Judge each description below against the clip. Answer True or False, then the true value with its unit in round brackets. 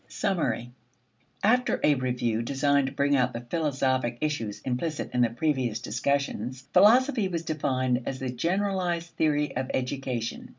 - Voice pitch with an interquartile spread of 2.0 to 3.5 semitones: False (4.4 semitones)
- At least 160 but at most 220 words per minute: False (140 wpm)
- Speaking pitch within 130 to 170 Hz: True (135 Hz)